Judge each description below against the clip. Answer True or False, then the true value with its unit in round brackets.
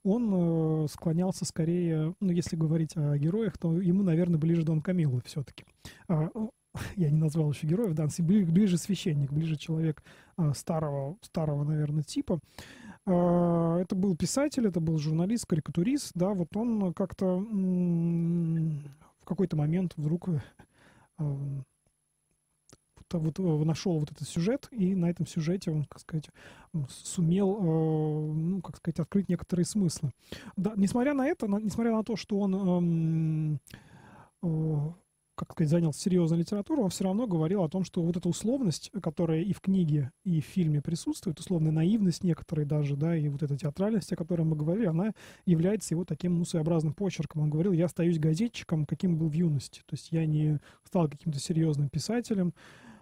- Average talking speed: True (150 wpm)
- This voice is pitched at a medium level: True (170 Hz)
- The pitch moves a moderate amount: True (3.0 semitones)